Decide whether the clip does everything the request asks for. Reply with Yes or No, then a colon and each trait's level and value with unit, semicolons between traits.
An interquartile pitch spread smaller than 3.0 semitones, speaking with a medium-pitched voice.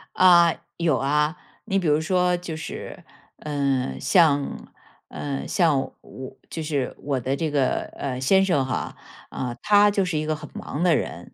No: average, 4.2 semitones; medium, 155 Hz